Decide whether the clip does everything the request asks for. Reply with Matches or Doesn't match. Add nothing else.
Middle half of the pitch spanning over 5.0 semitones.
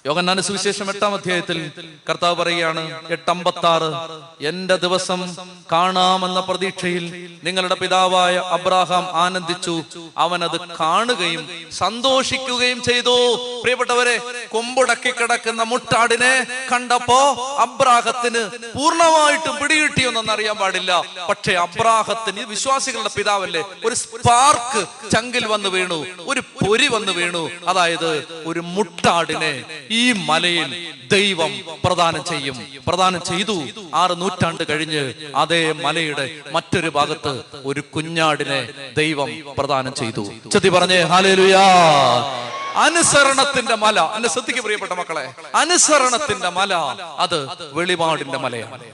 Matches